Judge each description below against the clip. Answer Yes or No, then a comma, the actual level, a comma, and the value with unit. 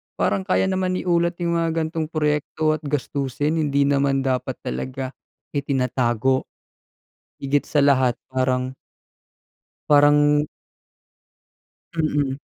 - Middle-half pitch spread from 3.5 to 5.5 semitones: No, average, 3.0 semitones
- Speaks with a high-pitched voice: No, medium, 145 Hz